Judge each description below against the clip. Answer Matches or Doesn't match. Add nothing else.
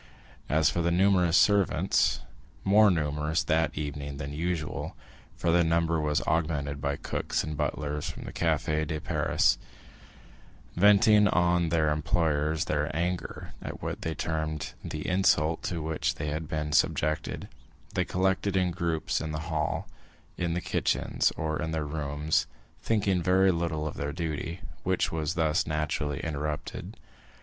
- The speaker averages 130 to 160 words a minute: Matches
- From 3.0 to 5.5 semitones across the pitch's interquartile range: Doesn't match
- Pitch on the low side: Matches